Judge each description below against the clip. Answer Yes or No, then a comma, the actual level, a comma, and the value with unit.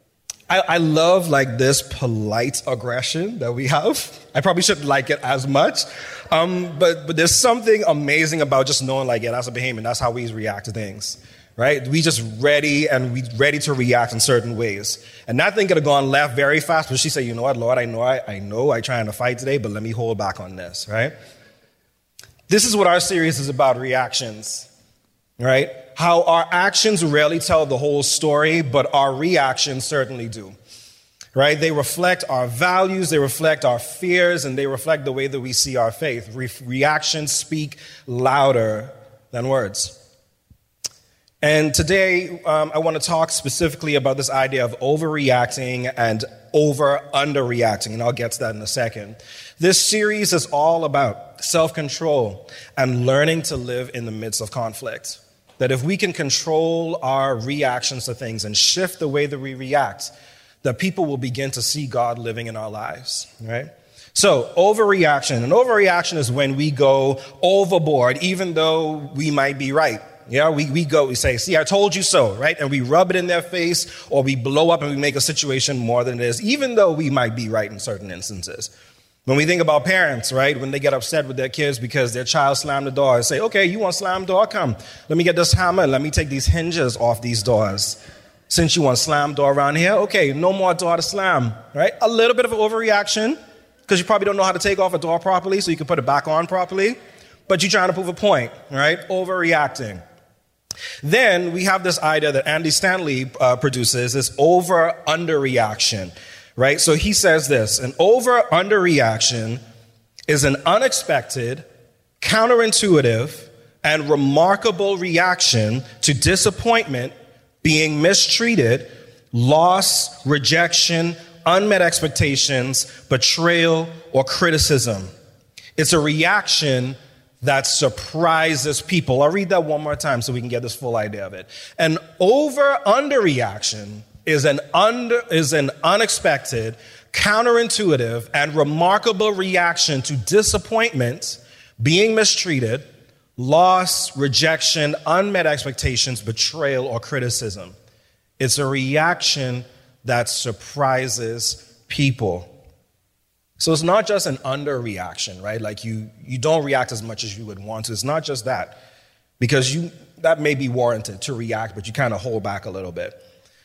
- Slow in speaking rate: No, average, 175 wpm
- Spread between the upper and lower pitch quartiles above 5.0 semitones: Yes, wide, 5.4 semitones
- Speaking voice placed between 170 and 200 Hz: No, medium, 140 Hz